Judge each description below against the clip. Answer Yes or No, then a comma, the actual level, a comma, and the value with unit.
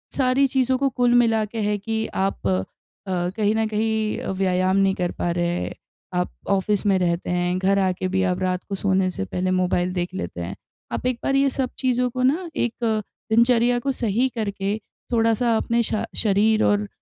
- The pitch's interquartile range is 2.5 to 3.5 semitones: No, average, 4.2 semitones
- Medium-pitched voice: No, high, 210 Hz